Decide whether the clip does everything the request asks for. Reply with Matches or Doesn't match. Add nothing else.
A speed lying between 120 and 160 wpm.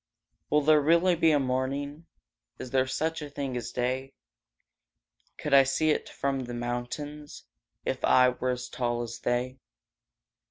Matches